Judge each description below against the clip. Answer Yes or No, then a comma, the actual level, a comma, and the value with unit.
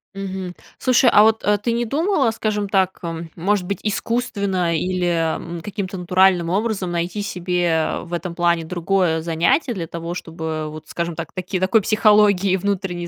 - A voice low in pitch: No, medium, 185 Hz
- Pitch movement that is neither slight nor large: Yes, average, 3.3 semitones